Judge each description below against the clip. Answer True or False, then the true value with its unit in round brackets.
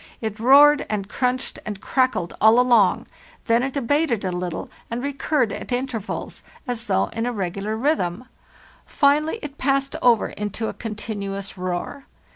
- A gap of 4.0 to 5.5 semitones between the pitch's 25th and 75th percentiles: True (4.8 semitones)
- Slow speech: False (150 wpm)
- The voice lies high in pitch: True (230 Hz)